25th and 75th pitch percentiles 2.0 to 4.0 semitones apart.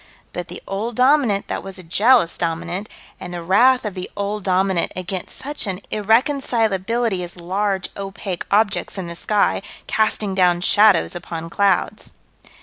Yes: average, 3.2 semitones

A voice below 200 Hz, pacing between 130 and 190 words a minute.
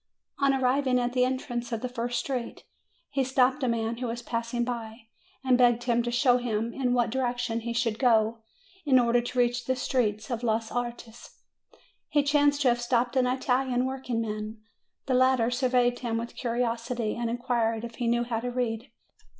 No: high, 240 Hz; average, 185 wpm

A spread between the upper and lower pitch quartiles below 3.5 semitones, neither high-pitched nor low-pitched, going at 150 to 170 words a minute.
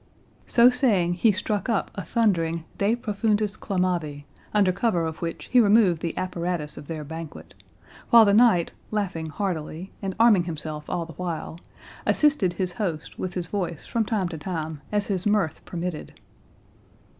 No: average, 4.1 semitones; medium, 180 Hz; average, 160 wpm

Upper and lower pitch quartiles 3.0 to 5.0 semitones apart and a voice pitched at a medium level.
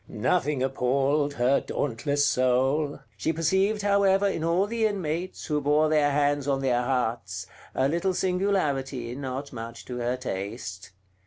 Yes: average, 4.7 semitones; medium, 145 Hz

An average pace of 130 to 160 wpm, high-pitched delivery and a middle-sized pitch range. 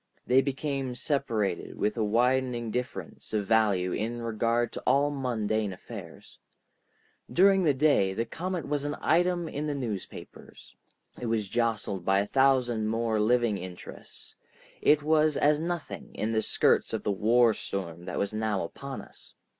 No: average, 155 wpm; low, 120 Hz; average, 4.6 semitones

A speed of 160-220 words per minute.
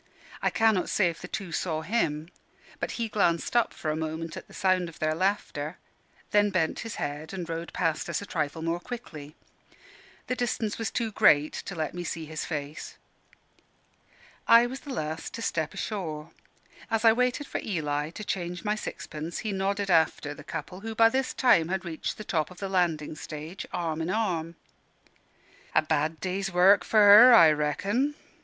Yes: average, 185 wpm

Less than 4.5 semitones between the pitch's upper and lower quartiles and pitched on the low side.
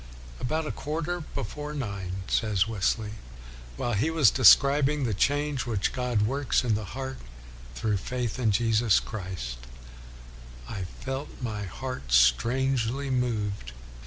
No: average, 5.0 semitones; low, 115 Hz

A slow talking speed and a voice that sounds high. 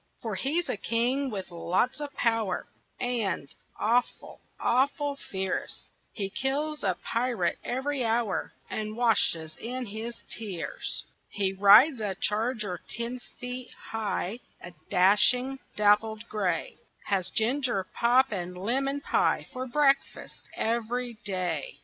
Yes: slow, 120 wpm; high, 225 Hz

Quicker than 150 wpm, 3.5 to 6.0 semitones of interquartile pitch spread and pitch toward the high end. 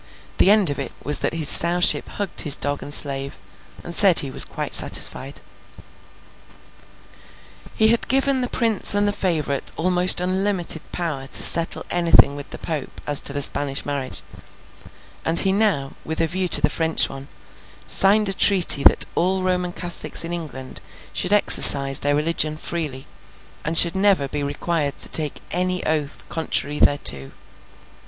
No: average, 160 wpm; average, 4.4 semitones; medium, 165 Hz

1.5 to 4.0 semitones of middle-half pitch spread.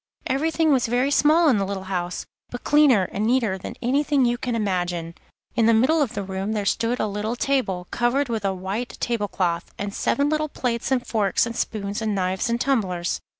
No: average, 5.0 semitones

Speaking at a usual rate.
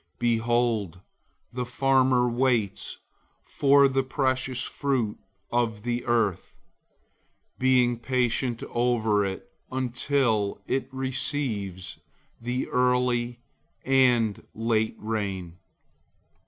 No: slow, 85 wpm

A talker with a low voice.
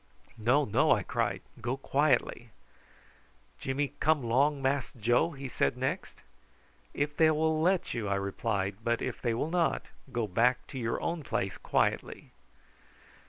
Yes: low, 130 Hz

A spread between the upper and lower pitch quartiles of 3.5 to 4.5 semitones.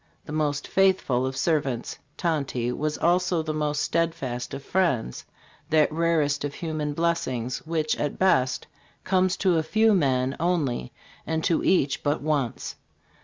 Yes: average, 3.8 semitones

